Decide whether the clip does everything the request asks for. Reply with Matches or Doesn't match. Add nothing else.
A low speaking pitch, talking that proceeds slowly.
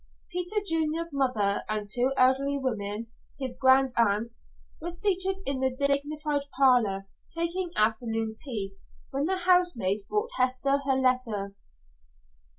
Doesn't match